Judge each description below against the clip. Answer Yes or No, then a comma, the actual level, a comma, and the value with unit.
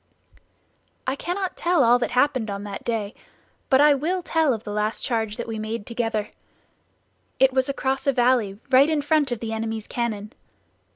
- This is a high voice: Yes, high, 245 Hz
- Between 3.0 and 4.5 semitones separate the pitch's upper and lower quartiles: Yes, average, 4.0 semitones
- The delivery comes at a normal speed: Yes, average, 180 wpm